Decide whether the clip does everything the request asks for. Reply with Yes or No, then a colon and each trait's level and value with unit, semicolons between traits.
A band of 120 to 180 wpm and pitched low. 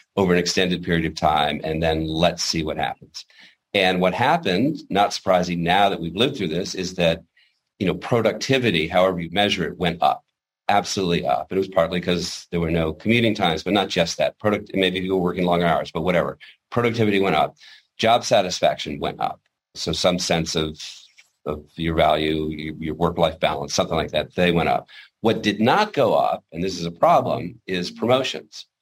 No: average, 195 wpm; very low, 90 Hz